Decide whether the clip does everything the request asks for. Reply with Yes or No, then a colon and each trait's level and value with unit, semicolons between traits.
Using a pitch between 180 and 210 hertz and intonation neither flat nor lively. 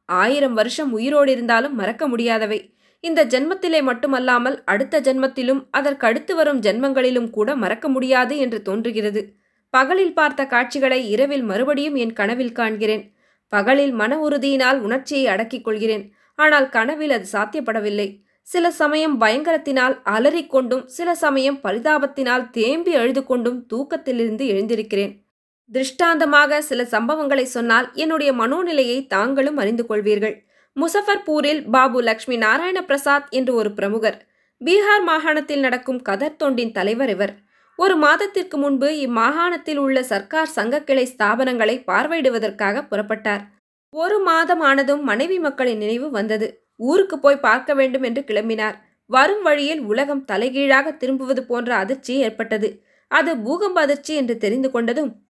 No: very high, 260 Hz; average, 4.7 semitones